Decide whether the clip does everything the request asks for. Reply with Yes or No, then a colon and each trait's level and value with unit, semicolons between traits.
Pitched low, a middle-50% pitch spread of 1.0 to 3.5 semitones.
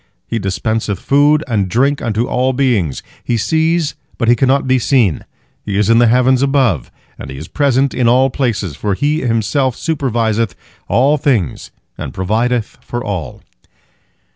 No: low, 120 Hz; average, 4.3 semitones